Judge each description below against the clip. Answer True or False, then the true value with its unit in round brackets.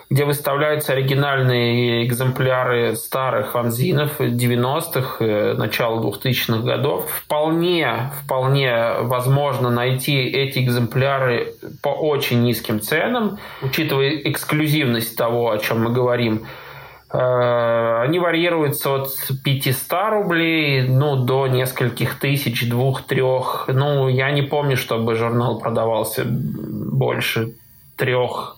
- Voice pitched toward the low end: True (130 Hz)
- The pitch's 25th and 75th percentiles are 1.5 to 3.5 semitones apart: True (2.8 semitones)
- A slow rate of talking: True (95 wpm)